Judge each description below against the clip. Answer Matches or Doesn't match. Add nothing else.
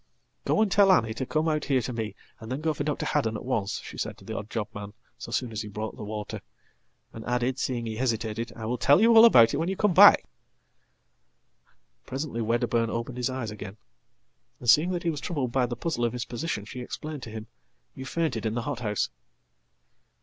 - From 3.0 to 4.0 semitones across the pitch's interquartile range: Doesn't match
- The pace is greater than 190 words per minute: Matches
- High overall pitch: Doesn't match